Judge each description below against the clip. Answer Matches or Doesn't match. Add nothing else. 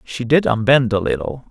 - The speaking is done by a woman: Doesn't match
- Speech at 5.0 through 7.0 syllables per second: Matches